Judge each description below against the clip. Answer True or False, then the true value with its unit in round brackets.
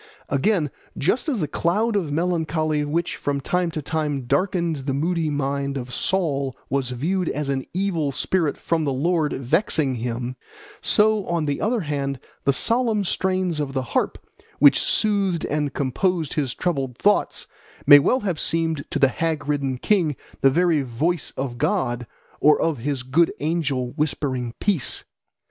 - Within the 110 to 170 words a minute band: True (160 wpm)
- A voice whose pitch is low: False (150 Hz)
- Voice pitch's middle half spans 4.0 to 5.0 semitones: True (4.3 semitones)